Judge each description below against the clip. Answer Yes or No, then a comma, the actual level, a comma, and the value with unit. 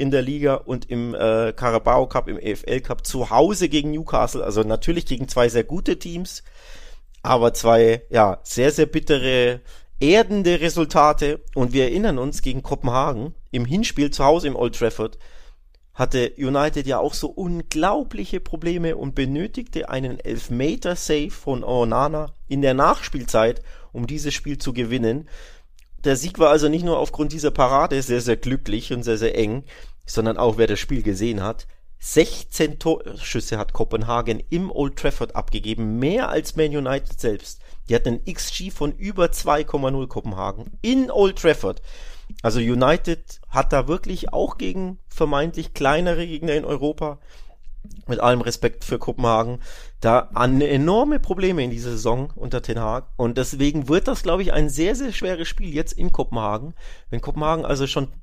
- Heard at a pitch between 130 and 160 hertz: Yes, medium, 140 Hz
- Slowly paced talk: No, average, 160 wpm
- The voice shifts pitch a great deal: No, average, 4.8 semitones